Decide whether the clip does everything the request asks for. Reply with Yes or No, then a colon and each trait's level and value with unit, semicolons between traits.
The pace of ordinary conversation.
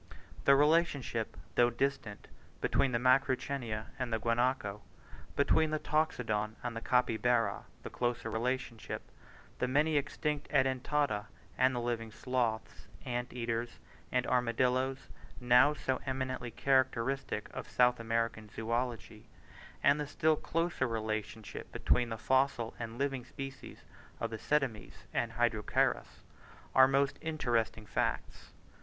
No: slow, 125 wpm